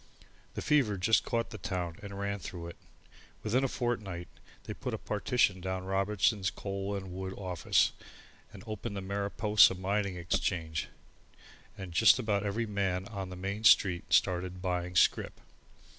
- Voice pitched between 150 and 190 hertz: No, low, 100 Hz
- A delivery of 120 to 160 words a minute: Yes, average, 155 wpm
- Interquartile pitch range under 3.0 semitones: Yes, narrow, 2.4 semitones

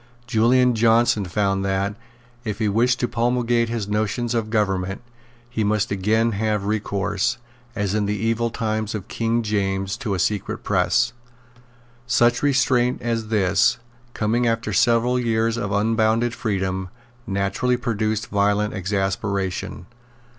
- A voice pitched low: Yes, low, 110 Hz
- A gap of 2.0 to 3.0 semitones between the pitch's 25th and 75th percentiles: Yes, average, 2.7 semitones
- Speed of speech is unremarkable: No, slow, 130 wpm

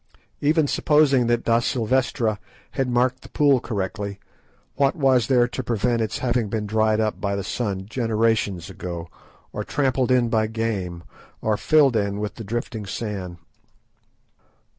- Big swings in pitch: No, average, 3.5 semitones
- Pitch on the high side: No, low, 115 Hz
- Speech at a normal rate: Yes, average, 145 wpm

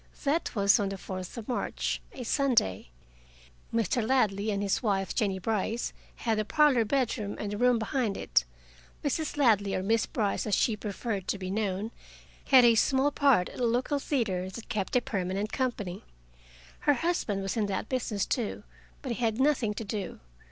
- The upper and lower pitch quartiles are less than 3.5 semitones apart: No, average, 4.0 semitones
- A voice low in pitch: No, high, 220 Hz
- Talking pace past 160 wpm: Yes, average, 180 wpm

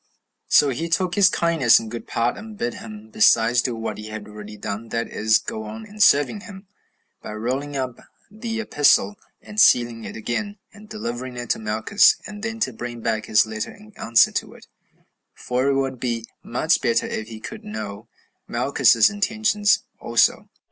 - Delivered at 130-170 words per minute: No, average, 185 wpm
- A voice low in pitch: Yes, low, 125 Hz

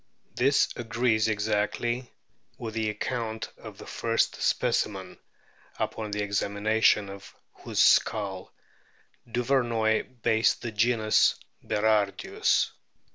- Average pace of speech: No, slow, 95 wpm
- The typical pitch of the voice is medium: No, low, 110 Hz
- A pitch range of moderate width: No, narrow, 2.2 semitones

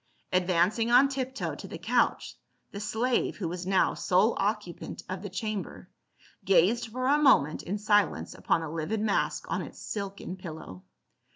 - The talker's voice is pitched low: No, high, 200 Hz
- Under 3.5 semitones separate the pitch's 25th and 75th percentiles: No, average, 3.8 semitones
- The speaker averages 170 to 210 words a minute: No, average, 160 wpm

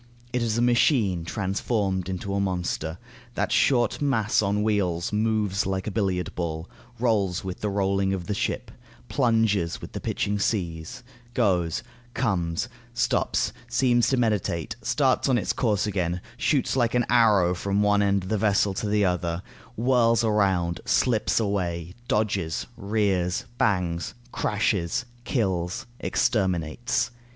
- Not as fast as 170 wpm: Yes, average, 140 wpm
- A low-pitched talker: Yes, low, 100 Hz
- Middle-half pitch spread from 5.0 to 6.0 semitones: No, average, 3.8 semitones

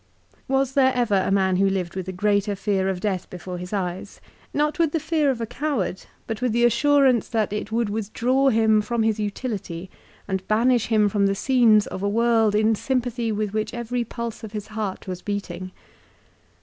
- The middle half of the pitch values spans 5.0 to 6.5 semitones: No, average, 3.5 semitones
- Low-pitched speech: No, high, 215 Hz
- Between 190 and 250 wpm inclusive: Yes, average, 200 wpm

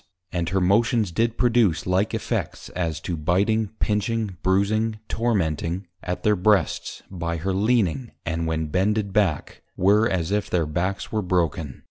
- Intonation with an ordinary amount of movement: Yes, average, 4.1 semitones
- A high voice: No, very low, 95 Hz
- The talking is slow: No, average, 150 wpm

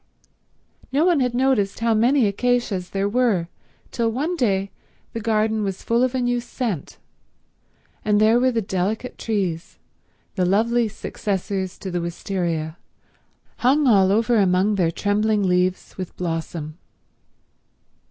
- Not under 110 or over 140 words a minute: Yes, slow, 135 wpm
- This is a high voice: Yes, high, 210 Hz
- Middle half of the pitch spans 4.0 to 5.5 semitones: Yes, average, 4.3 semitones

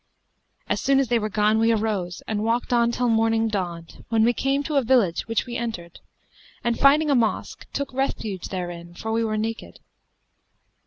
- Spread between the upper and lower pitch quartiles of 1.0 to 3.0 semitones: Yes, narrow, 2.6 semitones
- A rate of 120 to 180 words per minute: No, average, 190 wpm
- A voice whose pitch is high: Yes, high, 225 Hz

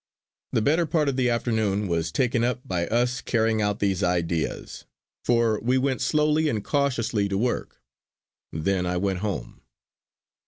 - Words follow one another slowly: No, average, 155 wpm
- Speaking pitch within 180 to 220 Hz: No, low, 110 Hz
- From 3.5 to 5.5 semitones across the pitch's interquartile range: Yes, average, 4.6 semitones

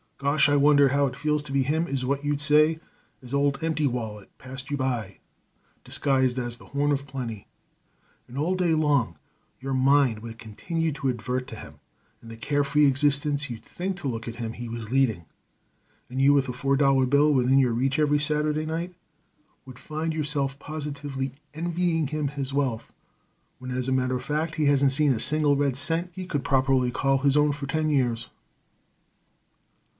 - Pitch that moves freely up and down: No, average, 2.7 semitones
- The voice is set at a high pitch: No, medium, 140 Hz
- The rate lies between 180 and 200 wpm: Yes, average, 190 wpm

